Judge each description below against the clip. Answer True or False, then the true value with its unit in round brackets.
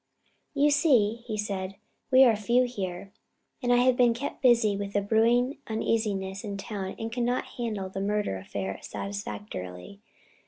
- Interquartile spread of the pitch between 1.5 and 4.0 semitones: True (3.6 semitones)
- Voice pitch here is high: True (215 Hz)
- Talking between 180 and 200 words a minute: False (155 wpm)